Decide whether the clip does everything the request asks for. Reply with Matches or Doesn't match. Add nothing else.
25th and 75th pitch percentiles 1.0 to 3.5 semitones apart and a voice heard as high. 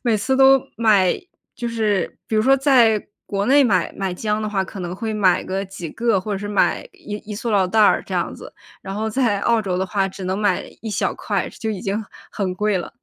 Matches